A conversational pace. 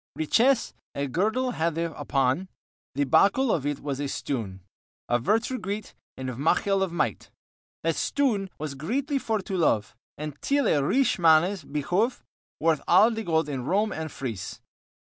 Yes: average, 160 wpm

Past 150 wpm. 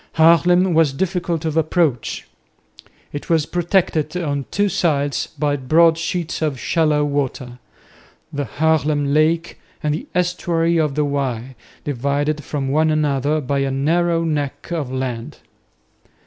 No: slow, 135 wpm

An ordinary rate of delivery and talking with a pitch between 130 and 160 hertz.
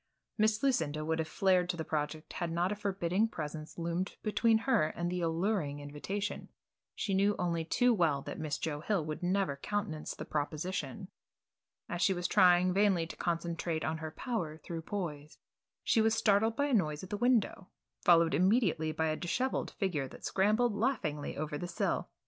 No: average, 180 wpm; medium, 175 Hz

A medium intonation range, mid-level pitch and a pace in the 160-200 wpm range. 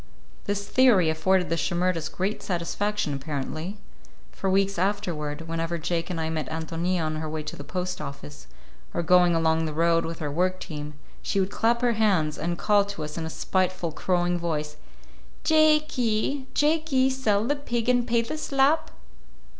Yes: average, 4.9 semitones; medium, 180 Hz; average, 180 wpm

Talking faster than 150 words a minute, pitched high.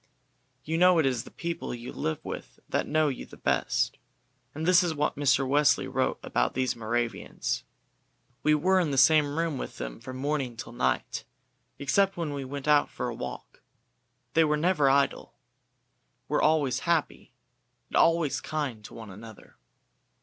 No: average, 170 wpm; medium, 145 Hz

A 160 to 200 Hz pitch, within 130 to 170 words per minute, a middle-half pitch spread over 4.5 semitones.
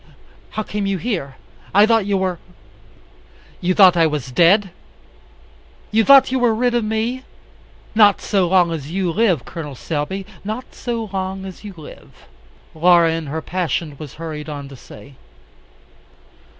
Yes: medium, 185 Hz; average, 160 wpm; average, 4.9 semitones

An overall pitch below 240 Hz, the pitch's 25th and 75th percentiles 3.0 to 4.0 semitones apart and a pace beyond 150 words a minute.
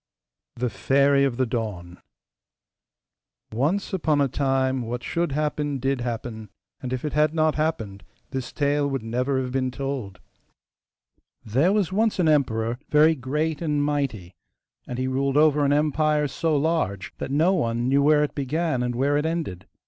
Yes: medium, 140 Hz; average, 3.6 semitones; average, 165 wpm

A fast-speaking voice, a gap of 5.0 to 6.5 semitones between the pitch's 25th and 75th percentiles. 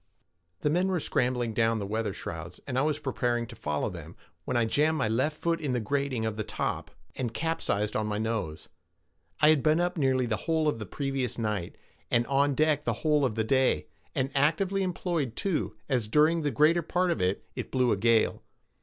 Yes: fast, 210 wpm; wide, 5.6 semitones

